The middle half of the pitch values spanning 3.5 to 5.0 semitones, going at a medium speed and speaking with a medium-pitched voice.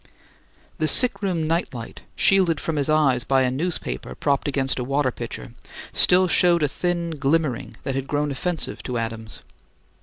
Yes: average, 4.3 semitones; average, 170 wpm; medium, 145 Hz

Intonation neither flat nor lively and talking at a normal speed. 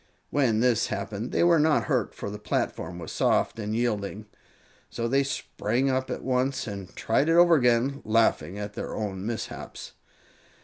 Yes: average, 4.3 semitones; average, 170 wpm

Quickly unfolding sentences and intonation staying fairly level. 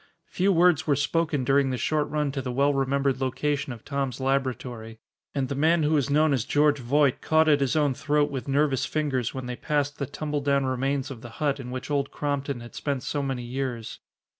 Yes: fast, 215 wpm; narrow, 2.1 semitones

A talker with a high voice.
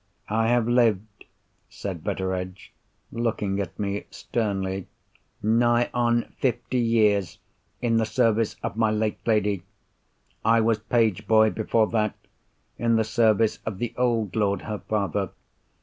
No: low, 110 Hz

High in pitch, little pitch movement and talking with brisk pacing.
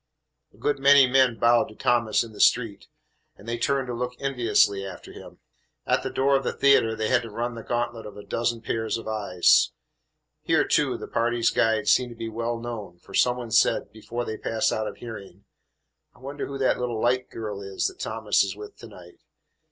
No: low, 115 Hz; narrow, 2.3 semitones; fast, 215 wpm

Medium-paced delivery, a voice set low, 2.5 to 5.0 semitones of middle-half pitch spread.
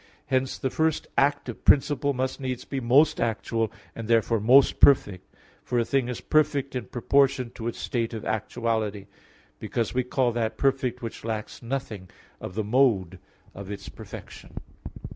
Yes: average, 160 wpm; low, 120 Hz; average, 3.2 semitones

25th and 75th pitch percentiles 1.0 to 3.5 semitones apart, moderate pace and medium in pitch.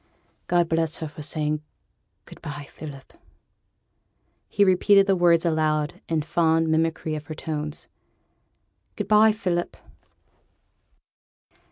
No: narrow, 2.4 semitones; slow, 115 wpm; medium, 160 Hz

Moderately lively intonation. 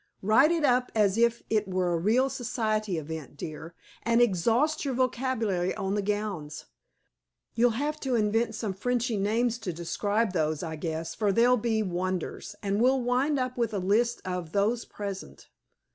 Yes: average, 4.5 semitones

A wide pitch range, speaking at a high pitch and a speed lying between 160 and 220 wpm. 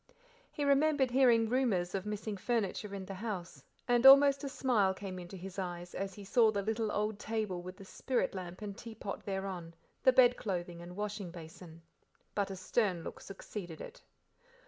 No: average, 3.9 semitones; high, 200 Hz; average, 180 wpm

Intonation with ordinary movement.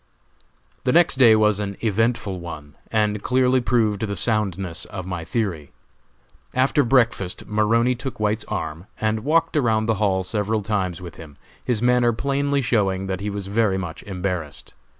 Yes: average, 3.9 semitones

